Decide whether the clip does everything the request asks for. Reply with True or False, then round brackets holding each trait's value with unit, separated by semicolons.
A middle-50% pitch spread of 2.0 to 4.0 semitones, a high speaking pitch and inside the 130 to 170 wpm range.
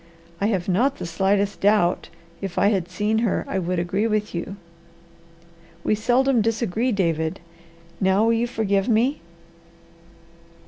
True (3.3 semitones; 205 Hz; 140 wpm)